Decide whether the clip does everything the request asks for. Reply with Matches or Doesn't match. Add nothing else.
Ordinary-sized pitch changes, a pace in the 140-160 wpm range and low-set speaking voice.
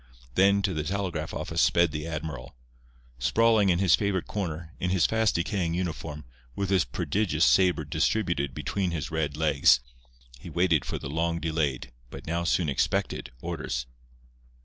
Matches